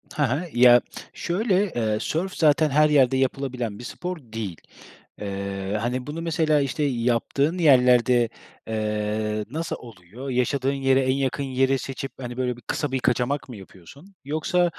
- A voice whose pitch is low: Yes, low, 130 Hz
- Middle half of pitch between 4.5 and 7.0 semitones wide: No, average, 4.1 semitones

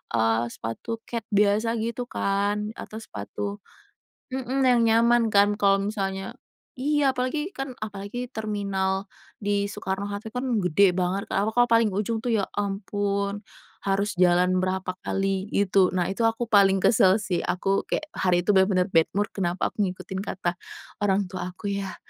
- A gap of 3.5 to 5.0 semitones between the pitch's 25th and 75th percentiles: No, narrow, 2.5 semitones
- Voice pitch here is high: Yes, high, 200 Hz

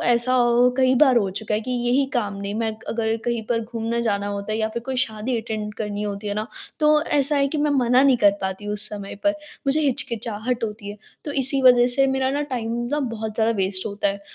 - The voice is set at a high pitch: Yes, high, 235 Hz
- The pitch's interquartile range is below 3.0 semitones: No, average, 3.6 semitones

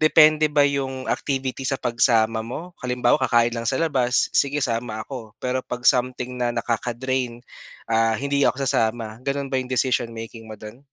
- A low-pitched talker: Yes, low, 125 Hz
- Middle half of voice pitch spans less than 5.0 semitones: Yes, narrow, 2.6 semitones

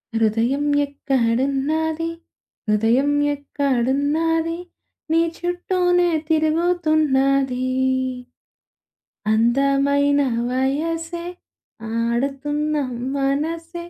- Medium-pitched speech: No, very high, 285 Hz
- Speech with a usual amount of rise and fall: Yes, average, 3.5 semitones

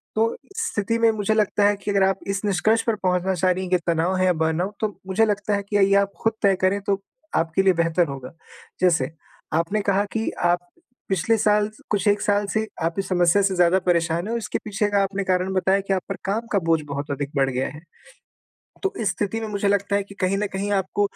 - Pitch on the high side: Yes, high, 195 Hz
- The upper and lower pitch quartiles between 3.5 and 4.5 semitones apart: No, narrow, 2.4 semitones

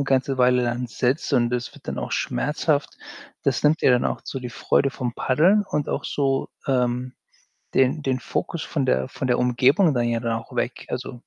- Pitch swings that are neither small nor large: No, narrow, 2.1 semitones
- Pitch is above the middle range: No, low, 125 Hz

